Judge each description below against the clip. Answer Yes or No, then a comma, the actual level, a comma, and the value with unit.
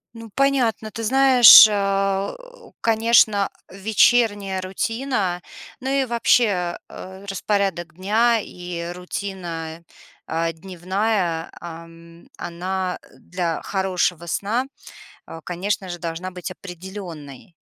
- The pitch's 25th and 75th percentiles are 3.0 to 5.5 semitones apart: Yes, average, 3.9 semitones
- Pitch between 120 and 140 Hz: No, high, 190 Hz